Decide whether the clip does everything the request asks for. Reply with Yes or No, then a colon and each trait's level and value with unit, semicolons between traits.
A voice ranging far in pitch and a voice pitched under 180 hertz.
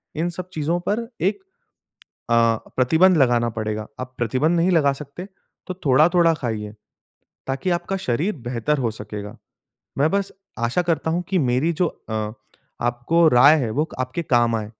Yes: wide, 6.2 semitones; medium, 140 Hz